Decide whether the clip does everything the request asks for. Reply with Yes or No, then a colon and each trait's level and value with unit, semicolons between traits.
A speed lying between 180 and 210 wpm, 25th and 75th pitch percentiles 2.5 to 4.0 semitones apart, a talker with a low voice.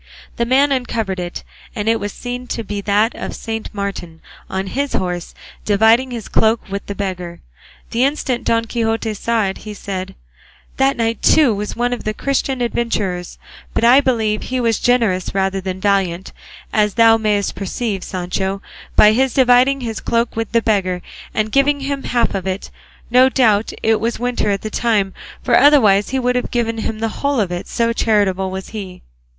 No: average, 185 wpm; average, 3.7 semitones; high, 220 Hz